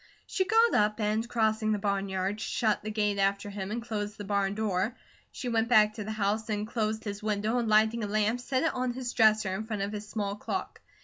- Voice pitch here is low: No, high, 215 Hz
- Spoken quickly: Yes, fast, 230 wpm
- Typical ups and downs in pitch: No, narrow, 1.7 semitones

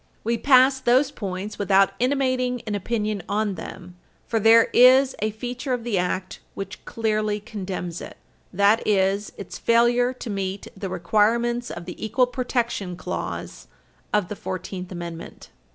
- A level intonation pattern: No, average, 3.9 semitones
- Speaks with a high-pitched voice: Yes, high, 215 Hz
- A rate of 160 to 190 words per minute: No, average, 150 wpm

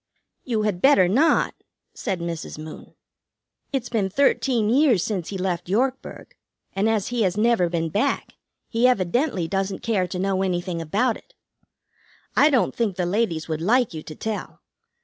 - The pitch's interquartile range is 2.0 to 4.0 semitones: No, average, 5.1 semitones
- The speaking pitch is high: Yes, high, 200 Hz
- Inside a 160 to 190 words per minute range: Yes, average, 165 wpm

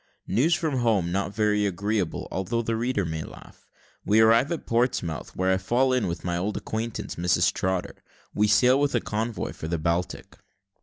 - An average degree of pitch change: Yes, average, 4.8 semitones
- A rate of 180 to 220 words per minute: Yes, average, 185 wpm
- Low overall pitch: Yes, low, 105 Hz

